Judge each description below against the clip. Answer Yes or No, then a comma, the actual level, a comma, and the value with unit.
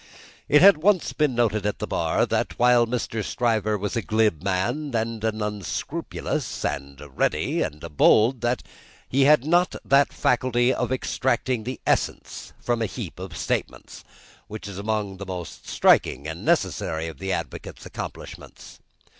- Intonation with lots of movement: No, average, 4.5 semitones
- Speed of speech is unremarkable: Yes, average, 160 wpm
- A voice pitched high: No, low, 110 Hz